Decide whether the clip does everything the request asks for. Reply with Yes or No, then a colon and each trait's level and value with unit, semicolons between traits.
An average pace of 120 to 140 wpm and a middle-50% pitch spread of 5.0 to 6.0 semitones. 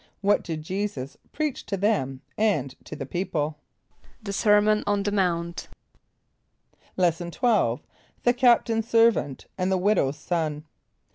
Yes: slow, 135 wpm; wide, 5.4 semitones